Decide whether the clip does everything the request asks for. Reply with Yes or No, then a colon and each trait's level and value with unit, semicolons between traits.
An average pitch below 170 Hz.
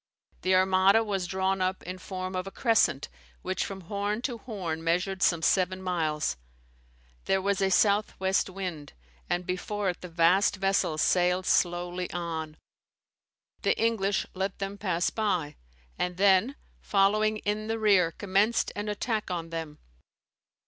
No: high, 190 Hz